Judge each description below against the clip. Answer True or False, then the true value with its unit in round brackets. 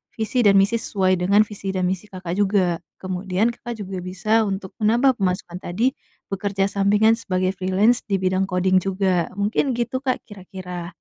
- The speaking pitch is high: True (195 Hz)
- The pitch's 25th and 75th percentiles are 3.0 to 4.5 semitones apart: False (2.5 semitones)